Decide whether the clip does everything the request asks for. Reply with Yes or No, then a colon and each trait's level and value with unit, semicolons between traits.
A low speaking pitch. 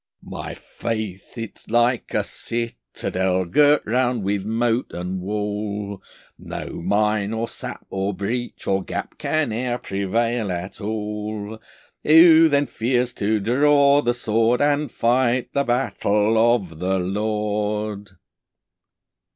Yes: low, 110 Hz